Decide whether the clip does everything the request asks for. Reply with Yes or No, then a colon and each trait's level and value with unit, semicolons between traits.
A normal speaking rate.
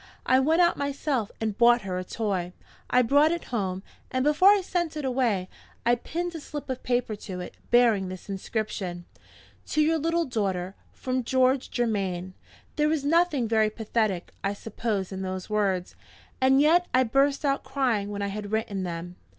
Yes: average, 180 wpm